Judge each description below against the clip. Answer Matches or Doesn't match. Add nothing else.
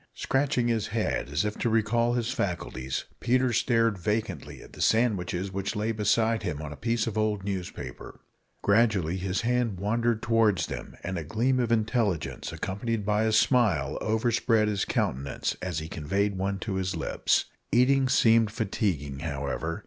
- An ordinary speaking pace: Matches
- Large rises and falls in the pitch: Doesn't match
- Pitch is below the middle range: Matches